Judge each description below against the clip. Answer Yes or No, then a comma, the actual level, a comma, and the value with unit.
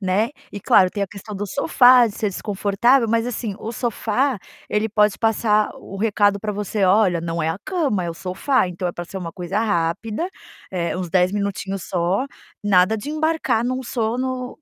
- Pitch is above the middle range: Yes, high, 210 Hz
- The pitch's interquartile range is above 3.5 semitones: Yes, average, 4.0 semitones